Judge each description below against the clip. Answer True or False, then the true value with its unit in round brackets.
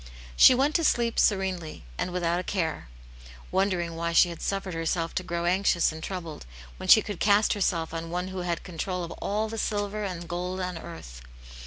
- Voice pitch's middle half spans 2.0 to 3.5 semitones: True (2.9 semitones)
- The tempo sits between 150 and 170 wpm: False (200 wpm)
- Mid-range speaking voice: True (180 Hz)